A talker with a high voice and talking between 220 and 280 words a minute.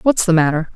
No: medium, 175 Hz; fast, 235 wpm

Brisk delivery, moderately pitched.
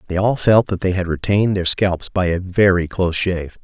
No: fast, 230 wpm; very low, 95 Hz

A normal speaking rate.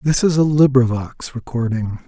Yes: average, 145 wpm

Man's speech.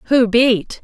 No: female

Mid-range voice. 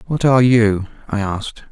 No: low, 110 Hz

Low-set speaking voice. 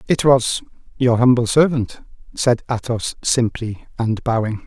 Yes: low, 120 Hz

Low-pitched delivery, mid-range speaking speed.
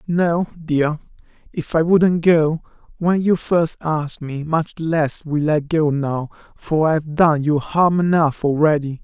No: medium, 155 Hz; average, 160 wpm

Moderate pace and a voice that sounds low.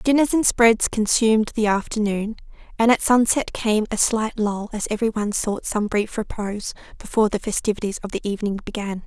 No: average, 170 wpm; high, 215 Hz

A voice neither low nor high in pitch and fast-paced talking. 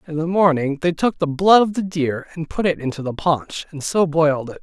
Yes: medium, 160 Hz; fast, 260 wpm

